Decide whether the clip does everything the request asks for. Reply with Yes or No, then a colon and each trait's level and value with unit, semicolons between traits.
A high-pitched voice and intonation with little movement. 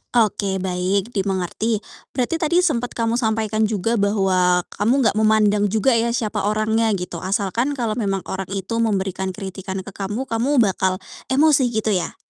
No: high, 215 Hz; average, 3.2 semitones